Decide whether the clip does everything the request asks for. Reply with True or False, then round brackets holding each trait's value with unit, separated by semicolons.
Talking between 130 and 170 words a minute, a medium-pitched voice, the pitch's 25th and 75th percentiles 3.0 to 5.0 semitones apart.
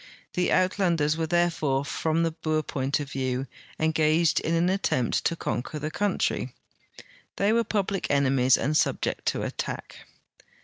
True (160 wpm; 160 Hz; 3.6 semitones)